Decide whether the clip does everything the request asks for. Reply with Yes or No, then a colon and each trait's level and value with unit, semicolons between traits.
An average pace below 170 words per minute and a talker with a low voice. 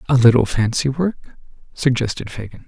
Yes: slow, 135 wpm; low, 125 Hz